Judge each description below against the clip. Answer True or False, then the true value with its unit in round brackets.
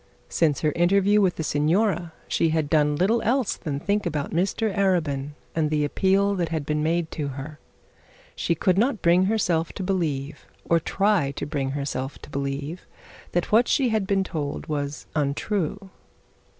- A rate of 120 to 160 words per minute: False (170 wpm)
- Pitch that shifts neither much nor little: True (4.8 semitones)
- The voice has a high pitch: False (165 Hz)